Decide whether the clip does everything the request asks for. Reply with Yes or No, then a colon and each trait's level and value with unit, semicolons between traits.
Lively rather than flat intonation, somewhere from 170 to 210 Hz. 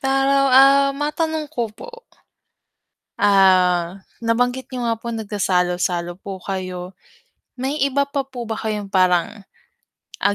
No: wide, 6.4 semitones; high, 225 Hz